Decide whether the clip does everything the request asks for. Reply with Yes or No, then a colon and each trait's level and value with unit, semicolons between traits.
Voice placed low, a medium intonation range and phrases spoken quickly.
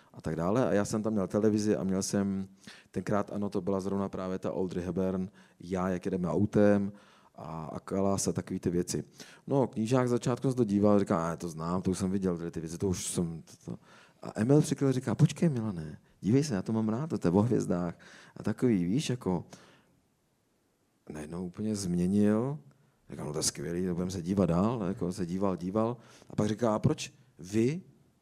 Yes: low, 100 Hz; average, 3.2 semitones; fast, 215 wpm